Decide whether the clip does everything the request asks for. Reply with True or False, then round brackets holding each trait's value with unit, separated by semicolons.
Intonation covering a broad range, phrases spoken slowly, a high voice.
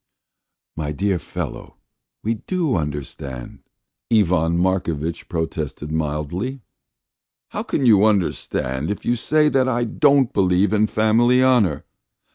False (7.1 semitones; 115 wpm; 100 Hz)